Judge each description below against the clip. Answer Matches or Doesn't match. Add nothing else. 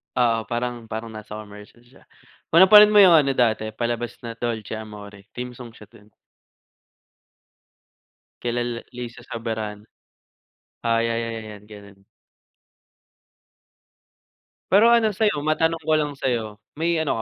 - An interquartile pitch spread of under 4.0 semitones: Doesn't match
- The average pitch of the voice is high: Doesn't match